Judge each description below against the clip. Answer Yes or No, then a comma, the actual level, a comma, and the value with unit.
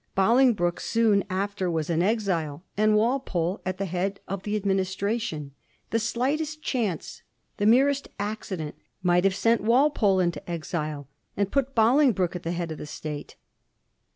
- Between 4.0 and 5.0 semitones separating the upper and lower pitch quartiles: Yes, average, 4.7 semitones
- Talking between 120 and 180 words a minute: Yes, average, 150 wpm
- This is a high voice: Yes, high, 200 Hz